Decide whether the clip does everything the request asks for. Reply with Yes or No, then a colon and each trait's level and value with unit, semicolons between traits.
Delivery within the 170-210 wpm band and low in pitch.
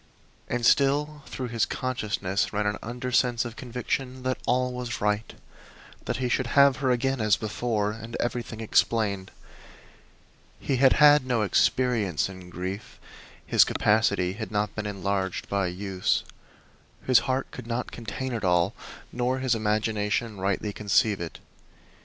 No: average, 145 wpm; low, 115 Hz